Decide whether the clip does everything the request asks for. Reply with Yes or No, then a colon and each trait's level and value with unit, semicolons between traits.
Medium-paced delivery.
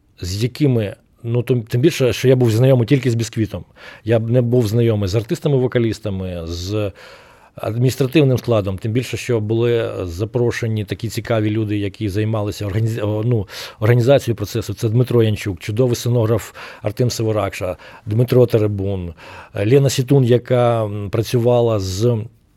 Yes: average, 135 wpm